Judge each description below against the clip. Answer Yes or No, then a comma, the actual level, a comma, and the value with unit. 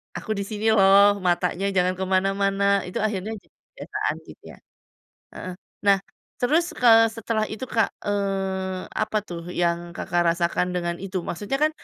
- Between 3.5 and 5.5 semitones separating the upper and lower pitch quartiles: No, average, 2.9 semitones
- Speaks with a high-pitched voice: Yes, high, 195 Hz